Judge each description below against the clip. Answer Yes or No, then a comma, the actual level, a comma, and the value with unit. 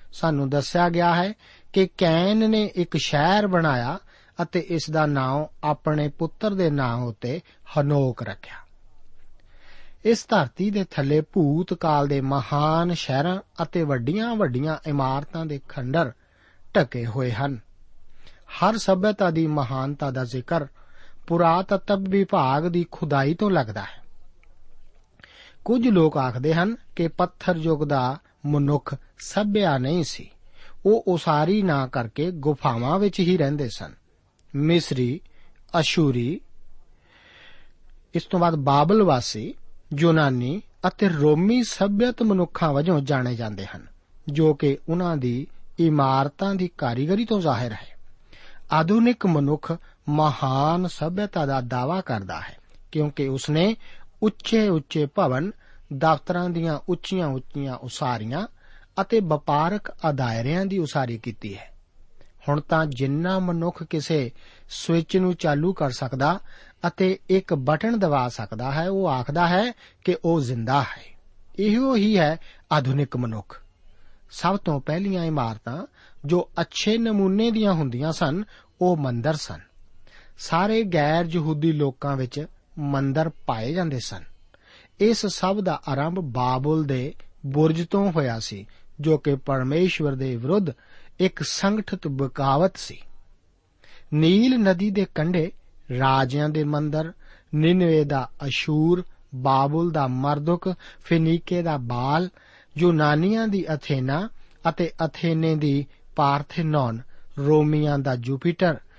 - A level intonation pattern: No, average, 5.0 semitones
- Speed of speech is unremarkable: Yes, average, 120 wpm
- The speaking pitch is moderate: Yes, medium, 155 Hz